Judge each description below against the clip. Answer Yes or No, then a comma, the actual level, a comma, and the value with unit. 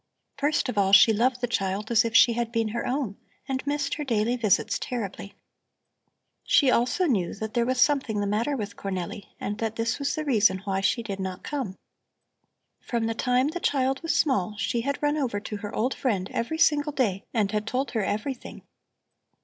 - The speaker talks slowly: No, average, 200 wpm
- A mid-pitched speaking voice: No, high, 230 Hz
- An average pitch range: Yes, average, 4.4 semitones